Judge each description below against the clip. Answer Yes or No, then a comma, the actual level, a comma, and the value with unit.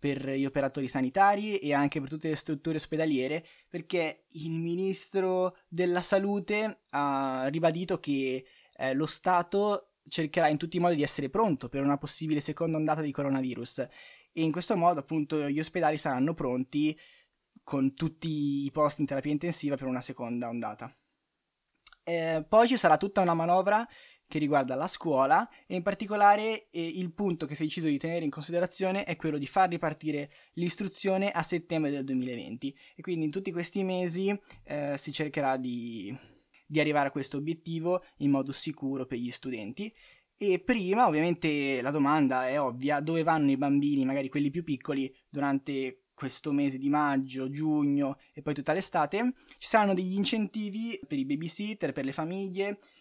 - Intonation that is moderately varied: Yes, average, 4.5 semitones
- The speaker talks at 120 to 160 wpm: No, fast, 170 wpm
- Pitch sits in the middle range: Yes, medium, 155 Hz